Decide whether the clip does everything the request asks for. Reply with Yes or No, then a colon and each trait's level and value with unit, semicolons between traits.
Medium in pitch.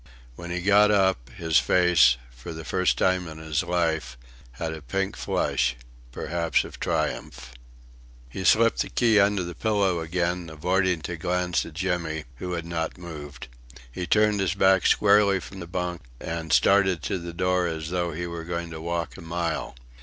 No: very low, 85 Hz